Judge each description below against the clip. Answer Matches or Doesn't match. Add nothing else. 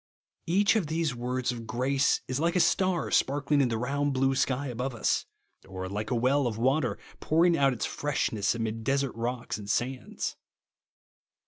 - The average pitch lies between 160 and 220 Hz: Doesn't match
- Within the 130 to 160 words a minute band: Doesn't match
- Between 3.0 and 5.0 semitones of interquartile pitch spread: Matches